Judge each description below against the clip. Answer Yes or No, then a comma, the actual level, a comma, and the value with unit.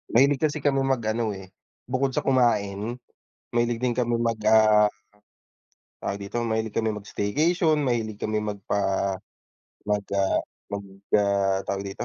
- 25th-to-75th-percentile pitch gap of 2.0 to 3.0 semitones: No, average, 3.4 semitones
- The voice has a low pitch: Yes, low, 110 Hz